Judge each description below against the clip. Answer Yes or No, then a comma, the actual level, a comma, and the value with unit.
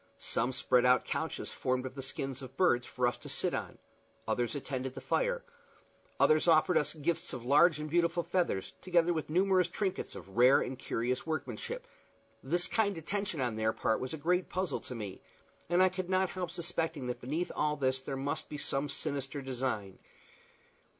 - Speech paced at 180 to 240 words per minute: Yes, average, 190 wpm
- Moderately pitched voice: Yes, medium, 145 Hz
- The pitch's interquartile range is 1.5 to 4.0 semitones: No, average, 5.3 semitones